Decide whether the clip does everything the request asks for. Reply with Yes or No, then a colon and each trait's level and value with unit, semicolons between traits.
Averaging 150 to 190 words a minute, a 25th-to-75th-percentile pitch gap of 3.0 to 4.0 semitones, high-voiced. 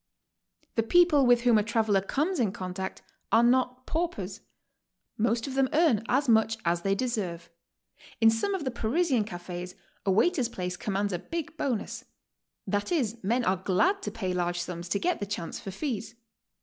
No: average, 180 wpm; average, 5.3 semitones; high, 225 Hz